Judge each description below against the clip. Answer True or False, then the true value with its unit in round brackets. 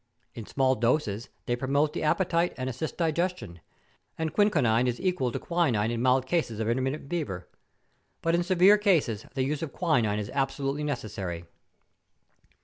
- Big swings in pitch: True (6.0 semitones)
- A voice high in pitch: False (135 Hz)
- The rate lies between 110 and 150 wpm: False (165 wpm)